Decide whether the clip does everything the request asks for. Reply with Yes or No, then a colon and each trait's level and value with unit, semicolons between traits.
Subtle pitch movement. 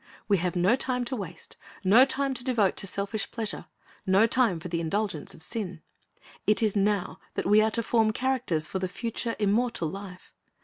No: average, 4.0 semitones